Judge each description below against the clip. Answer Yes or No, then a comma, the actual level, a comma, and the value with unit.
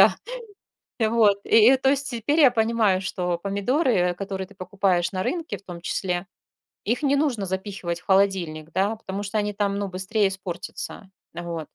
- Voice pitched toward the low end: No, high, 200 Hz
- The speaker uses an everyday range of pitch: Yes, average, 3.3 semitones